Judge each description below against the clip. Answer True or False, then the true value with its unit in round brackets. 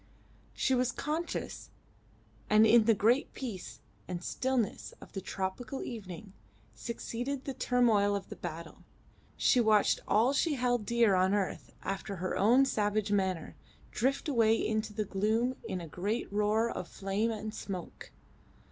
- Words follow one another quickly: False (145 wpm)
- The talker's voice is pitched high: True (215 Hz)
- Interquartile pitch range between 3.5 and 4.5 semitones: True (3.8 semitones)